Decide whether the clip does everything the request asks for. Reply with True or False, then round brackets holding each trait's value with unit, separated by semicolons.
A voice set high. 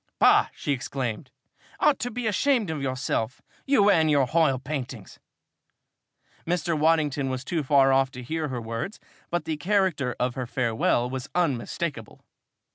False (140 Hz)